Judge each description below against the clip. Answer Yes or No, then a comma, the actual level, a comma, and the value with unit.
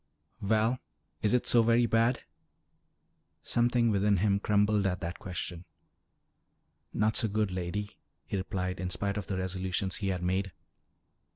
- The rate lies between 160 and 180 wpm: No, average, 145 wpm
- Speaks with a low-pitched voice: Yes, low, 100 Hz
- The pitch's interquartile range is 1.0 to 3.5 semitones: Yes, average, 2.8 semitones